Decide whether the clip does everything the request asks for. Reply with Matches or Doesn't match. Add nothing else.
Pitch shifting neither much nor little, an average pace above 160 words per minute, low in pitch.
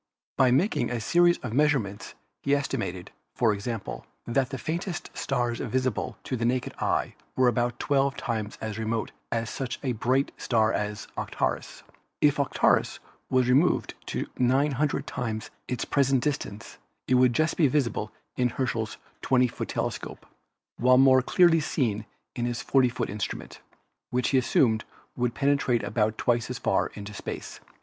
Doesn't match